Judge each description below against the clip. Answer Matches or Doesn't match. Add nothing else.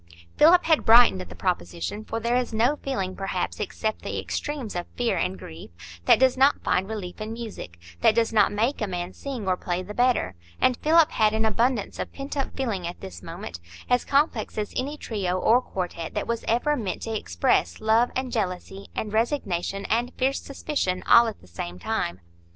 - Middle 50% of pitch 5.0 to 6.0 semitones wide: Matches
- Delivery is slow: Doesn't match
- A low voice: Doesn't match